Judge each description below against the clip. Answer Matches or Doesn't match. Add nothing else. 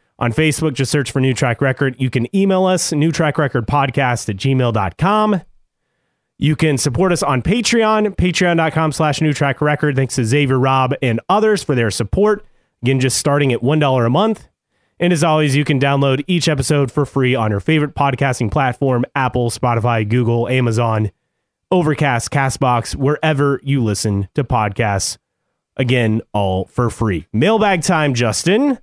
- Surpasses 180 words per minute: Doesn't match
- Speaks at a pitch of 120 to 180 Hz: Matches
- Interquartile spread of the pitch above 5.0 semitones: Doesn't match